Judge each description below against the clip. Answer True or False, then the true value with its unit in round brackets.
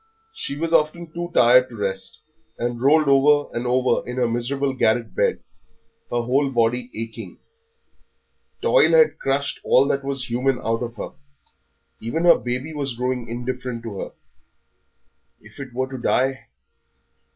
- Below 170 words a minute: True (150 wpm)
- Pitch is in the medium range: False (125 Hz)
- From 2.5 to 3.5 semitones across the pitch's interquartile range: True (2.8 semitones)